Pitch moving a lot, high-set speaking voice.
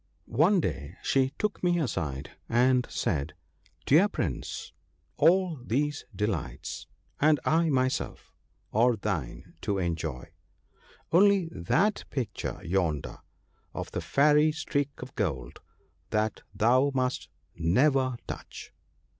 No: wide, 8.6 semitones; low, 125 Hz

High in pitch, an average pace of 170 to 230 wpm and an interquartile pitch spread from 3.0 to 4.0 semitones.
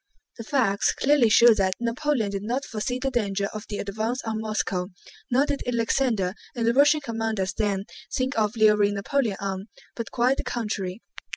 Yes: high, 225 Hz; average, 175 wpm; average, 3.7 semitones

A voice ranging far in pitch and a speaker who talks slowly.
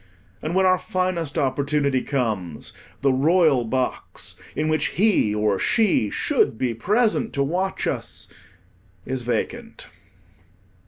Yes: wide, 6.7 semitones; slow, 120 wpm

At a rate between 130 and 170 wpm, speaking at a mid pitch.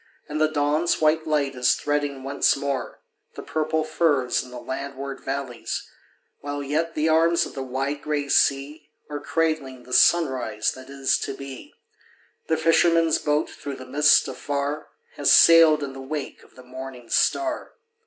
Yes: average, 165 wpm; medium, 145 Hz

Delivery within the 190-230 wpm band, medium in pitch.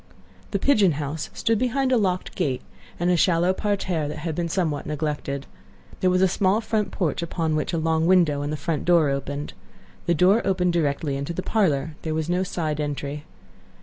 Yes: average, 195 wpm; medium, 165 Hz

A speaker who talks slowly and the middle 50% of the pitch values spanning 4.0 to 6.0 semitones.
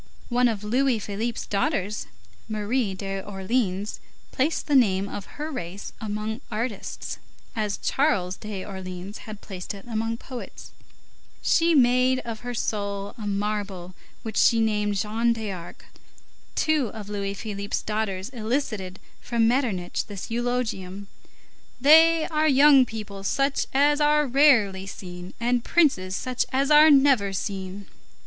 Yes: slow, 130 wpm; average, 4.4 semitones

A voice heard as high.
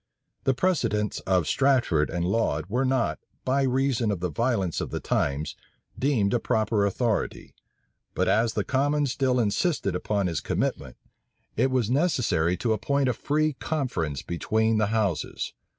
No: low, 115 Hz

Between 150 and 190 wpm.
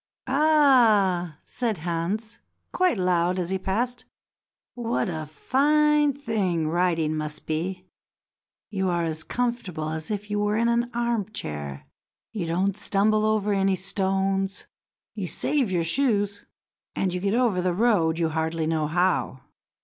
No: average, 140 wpm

